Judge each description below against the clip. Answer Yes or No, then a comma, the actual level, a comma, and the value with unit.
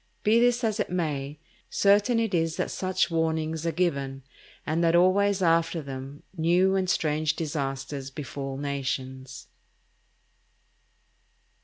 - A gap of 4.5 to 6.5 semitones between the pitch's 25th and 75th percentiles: Yes, average, 4.9 semitones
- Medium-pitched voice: Yes, medium, 160 Hz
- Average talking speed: No, slow, 125 wpm